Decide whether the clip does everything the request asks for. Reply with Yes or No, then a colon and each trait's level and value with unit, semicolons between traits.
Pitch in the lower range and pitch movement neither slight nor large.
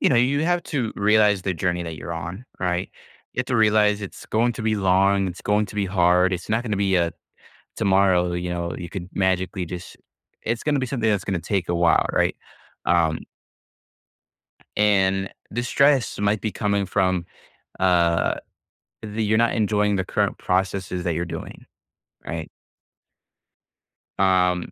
Yes: very low, 95 Hz; average, 3.2 semitones